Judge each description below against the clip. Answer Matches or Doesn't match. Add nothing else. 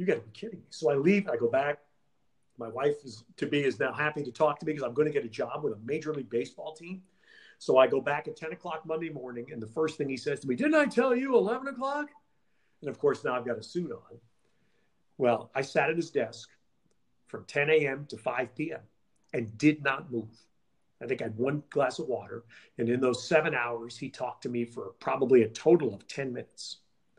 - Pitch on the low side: Doesn't match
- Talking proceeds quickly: Matches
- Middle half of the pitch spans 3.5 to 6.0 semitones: Matches